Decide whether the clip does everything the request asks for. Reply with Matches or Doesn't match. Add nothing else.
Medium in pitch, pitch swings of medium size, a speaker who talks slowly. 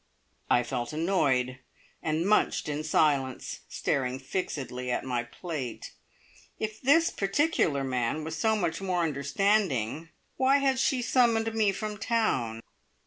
Doesn't match